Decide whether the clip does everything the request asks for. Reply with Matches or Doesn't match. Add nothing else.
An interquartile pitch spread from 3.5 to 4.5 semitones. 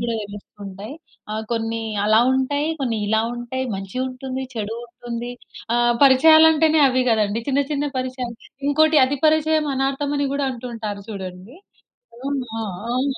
Matches